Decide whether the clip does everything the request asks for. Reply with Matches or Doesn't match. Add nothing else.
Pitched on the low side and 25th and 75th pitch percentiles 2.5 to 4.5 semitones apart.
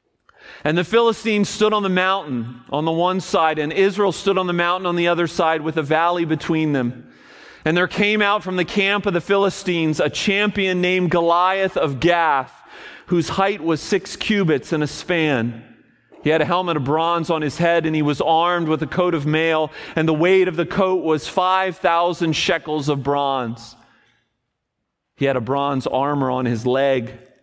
Doesn't match